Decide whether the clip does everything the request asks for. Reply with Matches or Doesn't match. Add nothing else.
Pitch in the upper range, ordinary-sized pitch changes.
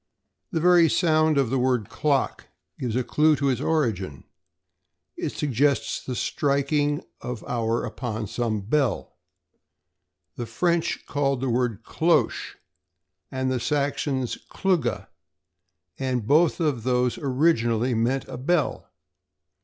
Doesn't match